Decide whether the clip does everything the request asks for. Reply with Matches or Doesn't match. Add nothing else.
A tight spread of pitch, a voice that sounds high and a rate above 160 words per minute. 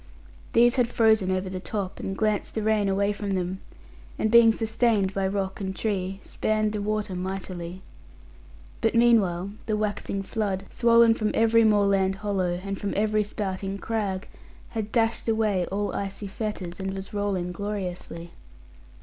Doesn't match